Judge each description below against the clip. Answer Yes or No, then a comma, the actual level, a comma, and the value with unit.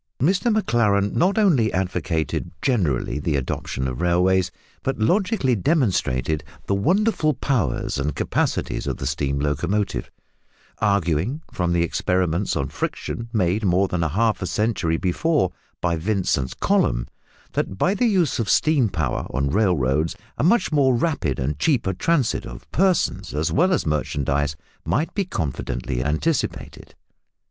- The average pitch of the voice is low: Yes, very low, 95 Hz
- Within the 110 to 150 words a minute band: Yes, average, 140 wpm